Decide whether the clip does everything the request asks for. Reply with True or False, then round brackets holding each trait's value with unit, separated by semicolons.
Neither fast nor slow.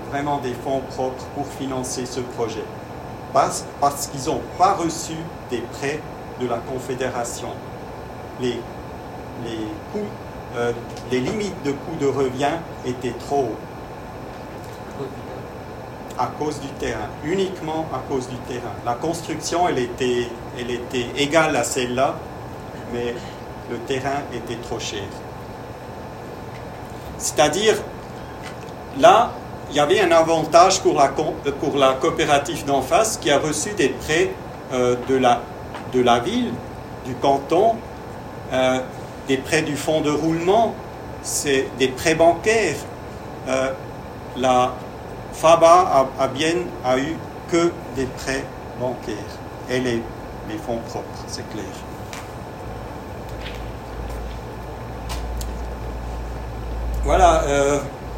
False (120 wpm)